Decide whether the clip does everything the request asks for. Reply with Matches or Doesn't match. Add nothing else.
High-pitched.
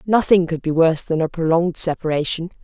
Doesn't match